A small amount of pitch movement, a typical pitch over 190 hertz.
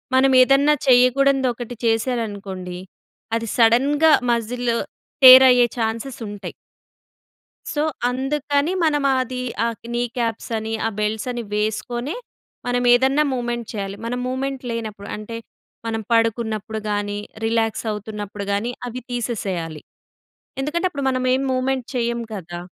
No: average, 3.1 semitones; high, 235 Hz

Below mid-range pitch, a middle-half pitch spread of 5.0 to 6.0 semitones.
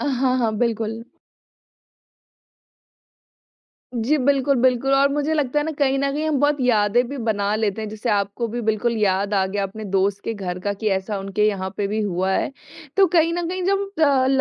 No: high, 230 Hz; wide, 5.5 semitones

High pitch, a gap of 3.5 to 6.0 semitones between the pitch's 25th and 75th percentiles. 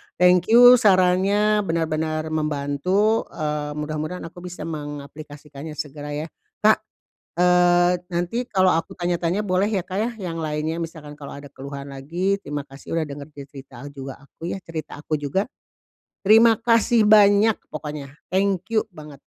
No: medium, 165 Hz; average, 4.4 semitones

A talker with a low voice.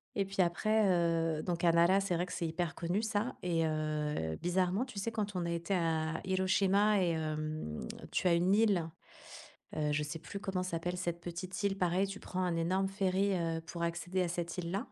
No: medium, 175 Hz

